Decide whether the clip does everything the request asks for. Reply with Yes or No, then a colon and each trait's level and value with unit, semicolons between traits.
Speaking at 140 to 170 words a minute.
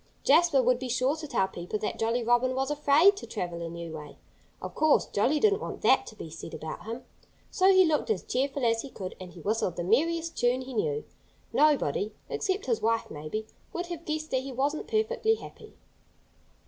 No: fast, 205 wpm